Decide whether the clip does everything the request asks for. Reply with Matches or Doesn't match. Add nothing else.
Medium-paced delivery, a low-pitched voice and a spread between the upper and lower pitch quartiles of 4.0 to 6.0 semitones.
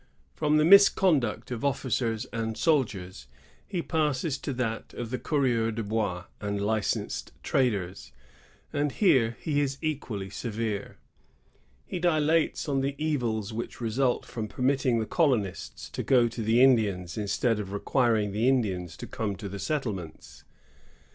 Matches